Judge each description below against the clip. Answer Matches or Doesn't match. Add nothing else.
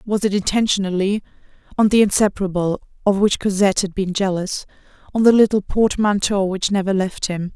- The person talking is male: Doesn't match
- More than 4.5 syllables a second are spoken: Matches